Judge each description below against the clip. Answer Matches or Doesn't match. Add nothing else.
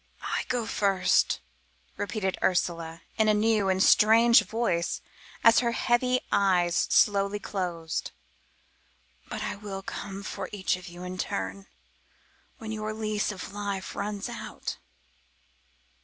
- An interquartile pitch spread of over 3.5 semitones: Doesn't match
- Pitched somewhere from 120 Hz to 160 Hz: Doesn't match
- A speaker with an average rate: Doesn't match